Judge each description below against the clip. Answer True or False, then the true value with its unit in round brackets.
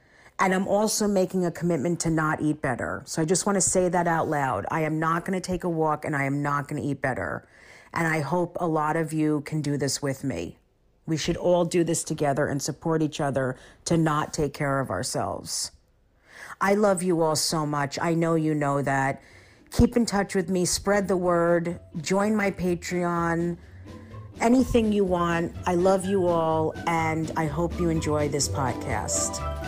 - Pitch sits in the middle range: True (160 Hz)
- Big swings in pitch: False (3.7 semitones)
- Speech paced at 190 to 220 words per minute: True (200 wpm)